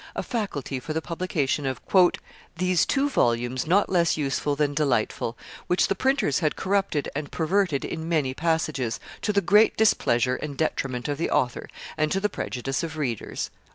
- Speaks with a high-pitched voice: No, medium, 155 Hz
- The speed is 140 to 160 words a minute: No, average, 170 wpm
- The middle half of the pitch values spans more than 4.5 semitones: Yes, average, 5.3 semitones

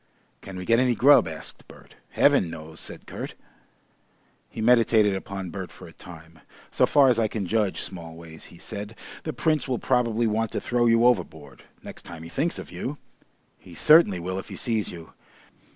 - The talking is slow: No, average, 185 wpm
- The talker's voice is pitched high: No, low, 105 Hz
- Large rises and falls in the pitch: Yes, wide, 5.8 semitones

